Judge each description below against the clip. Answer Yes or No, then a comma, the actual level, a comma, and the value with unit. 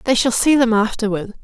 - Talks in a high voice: Yes, high, 225 Hz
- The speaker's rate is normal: No, fast, 210 wpm